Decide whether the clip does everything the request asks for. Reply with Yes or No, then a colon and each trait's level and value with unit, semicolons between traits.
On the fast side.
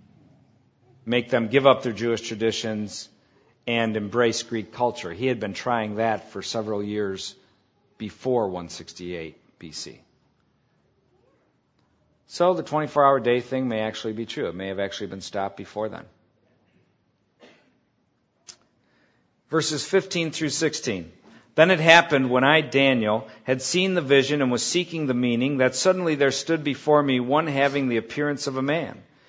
No: average, 150 wpm